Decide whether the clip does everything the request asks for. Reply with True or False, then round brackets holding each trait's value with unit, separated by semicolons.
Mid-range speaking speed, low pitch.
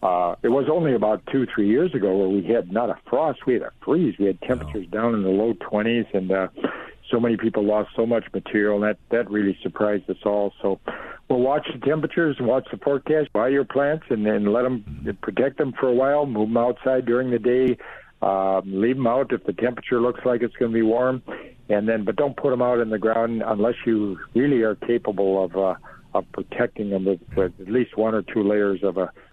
False (235 wpm; 115 Hz)